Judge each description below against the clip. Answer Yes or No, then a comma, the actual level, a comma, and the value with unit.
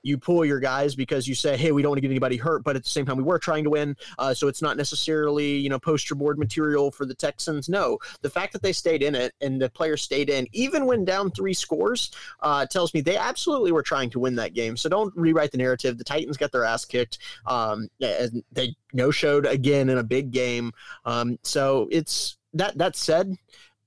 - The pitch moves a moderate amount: Yes, average, 3.7 semitones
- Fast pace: Yes, fast, 235 wpm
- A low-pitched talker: No, medium, 145 Hz